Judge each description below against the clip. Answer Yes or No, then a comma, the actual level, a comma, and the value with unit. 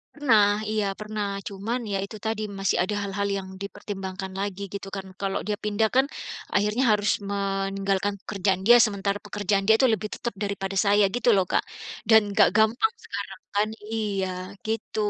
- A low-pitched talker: No, high, 205 Hz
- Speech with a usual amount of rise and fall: No, narrow, 1.7 semitones